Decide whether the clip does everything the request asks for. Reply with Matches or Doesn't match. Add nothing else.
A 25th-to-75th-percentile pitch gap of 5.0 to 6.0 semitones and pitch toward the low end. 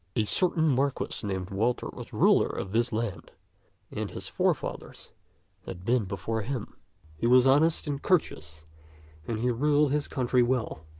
Matches